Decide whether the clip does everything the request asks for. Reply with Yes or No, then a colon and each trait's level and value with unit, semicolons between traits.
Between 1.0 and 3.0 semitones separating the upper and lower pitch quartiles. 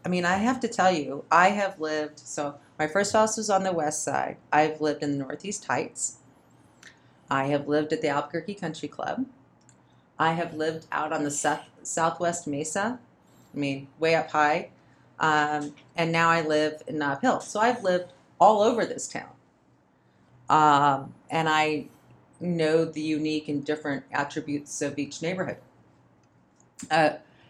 Yes: narrow, 2.6 semitones